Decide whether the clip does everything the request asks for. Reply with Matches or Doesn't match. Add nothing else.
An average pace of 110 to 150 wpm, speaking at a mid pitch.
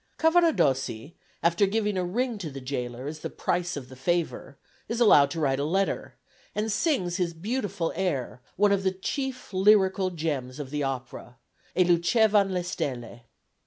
Doesn't match